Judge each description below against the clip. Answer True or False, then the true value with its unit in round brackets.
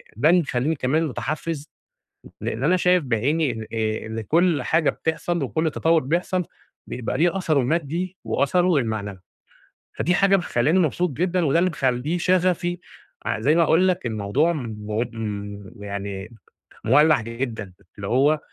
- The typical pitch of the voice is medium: True (150 Hz)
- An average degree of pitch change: False (7.1 semitones)